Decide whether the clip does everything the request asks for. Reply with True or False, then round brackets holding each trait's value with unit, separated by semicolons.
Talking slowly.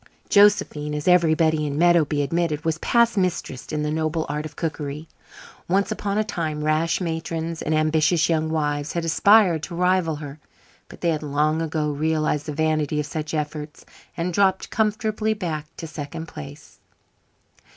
False (160 wpm)